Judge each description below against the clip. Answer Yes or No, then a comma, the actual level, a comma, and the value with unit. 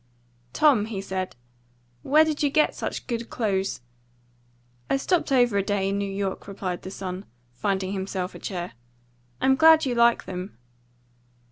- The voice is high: Yes, high, 200 Hz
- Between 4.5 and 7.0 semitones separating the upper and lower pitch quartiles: Yes, wide, 5.5 semitones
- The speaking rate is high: No, average, 155 wpm